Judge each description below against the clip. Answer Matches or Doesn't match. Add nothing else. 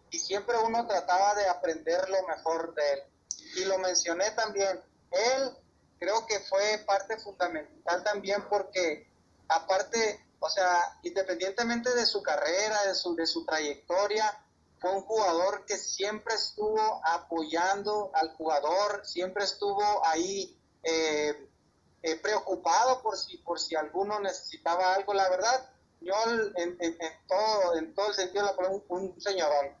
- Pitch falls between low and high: Doesn't match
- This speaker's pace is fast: Doesn't match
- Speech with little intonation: Doesn't match